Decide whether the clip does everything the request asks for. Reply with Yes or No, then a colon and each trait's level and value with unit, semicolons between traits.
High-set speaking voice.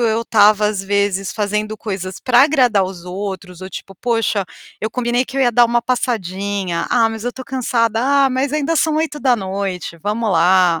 Yes: high, 215 Hz